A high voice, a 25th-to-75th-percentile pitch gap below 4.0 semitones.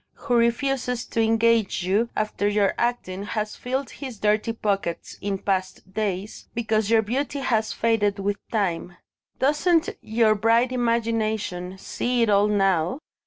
Yes: high, 220 Hz; average, 2.8 semitones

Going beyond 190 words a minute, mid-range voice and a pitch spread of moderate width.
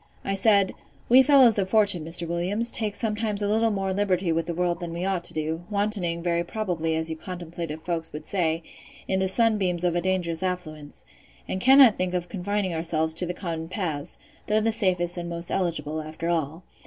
Yes: average, 200 wpm; medium, 180 Hz; average, 3.4 semitones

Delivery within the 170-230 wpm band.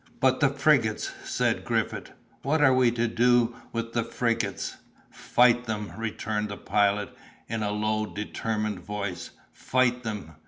No: average, 145 wpm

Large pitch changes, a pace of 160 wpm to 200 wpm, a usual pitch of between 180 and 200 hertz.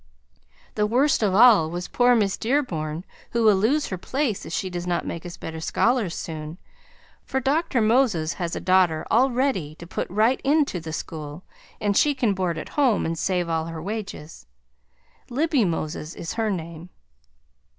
Yes: wide, 6.7 semitones; average, 180 wpm; high, 190 Hz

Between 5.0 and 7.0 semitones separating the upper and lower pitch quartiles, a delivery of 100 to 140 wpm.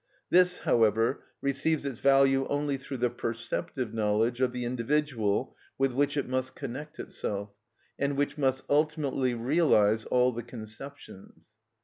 No: average, 3.4 semitones; slow, 135 wpm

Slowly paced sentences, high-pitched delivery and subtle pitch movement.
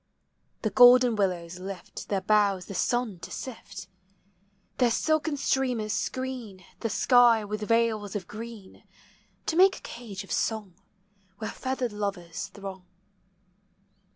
No: slow, 125 wpm; high, 215 Hz; average, 4.0 semitones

